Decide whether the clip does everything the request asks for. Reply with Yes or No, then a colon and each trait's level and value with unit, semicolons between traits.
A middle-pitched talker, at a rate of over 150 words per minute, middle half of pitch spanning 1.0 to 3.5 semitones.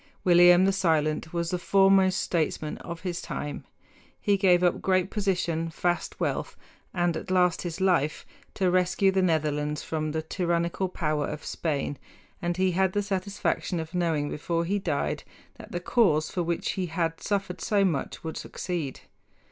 Yes: medium, 175 Hz; average, 165 wpm; average, 2.8 semitones